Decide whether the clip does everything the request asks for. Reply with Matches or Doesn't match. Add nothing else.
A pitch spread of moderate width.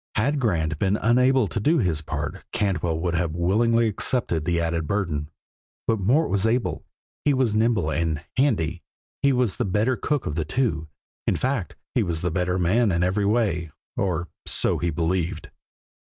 Doesn't match